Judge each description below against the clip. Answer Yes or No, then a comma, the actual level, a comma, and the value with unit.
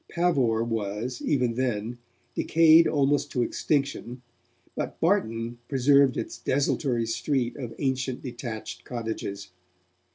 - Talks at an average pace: No, slow, 105 wpm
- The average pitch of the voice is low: Yes, low, 125 Hz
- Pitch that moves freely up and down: No, average, 3.4 semitones